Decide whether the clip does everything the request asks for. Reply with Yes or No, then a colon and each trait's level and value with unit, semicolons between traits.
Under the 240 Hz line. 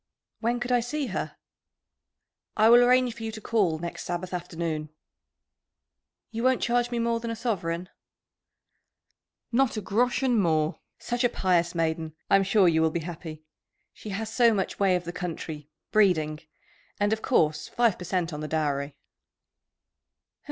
Yes: high, 190 Hz